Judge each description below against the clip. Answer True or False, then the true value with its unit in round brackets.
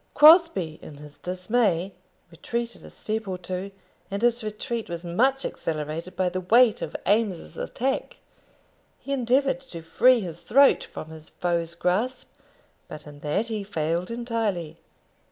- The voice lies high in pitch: True (195 Hz)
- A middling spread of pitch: False (5.8 semitones)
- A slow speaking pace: False (145 wpm)